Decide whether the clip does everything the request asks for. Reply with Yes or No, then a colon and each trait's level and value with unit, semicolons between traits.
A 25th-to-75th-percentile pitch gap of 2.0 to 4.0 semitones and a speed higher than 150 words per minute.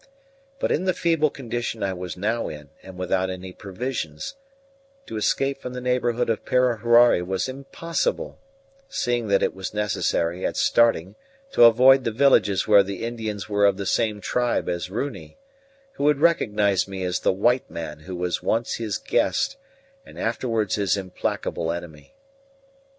No: average, 4.9 semitones; average, 160 wpm